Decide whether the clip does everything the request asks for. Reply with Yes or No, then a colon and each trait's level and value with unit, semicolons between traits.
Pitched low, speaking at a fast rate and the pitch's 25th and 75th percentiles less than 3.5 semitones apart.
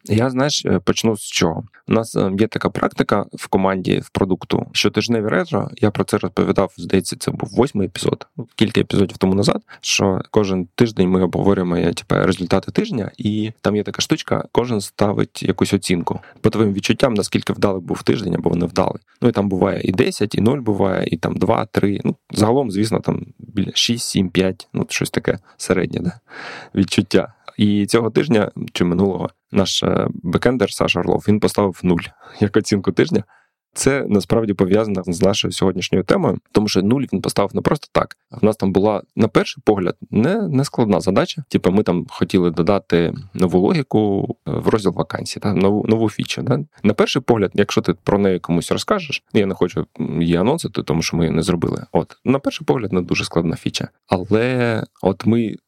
Yes: low, 100 Hz; fast, 185 wpm; average, 2.9 semitones